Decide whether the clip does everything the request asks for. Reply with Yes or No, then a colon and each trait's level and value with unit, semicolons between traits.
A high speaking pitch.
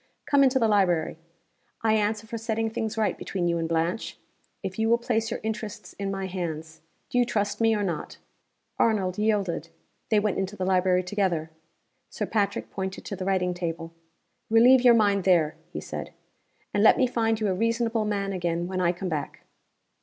Yes: high, 200 Hz